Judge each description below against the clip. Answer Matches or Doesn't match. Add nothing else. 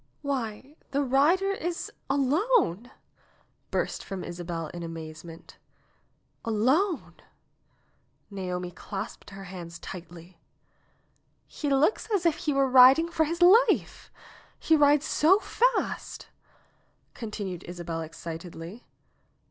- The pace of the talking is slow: Matches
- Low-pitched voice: Doesn't match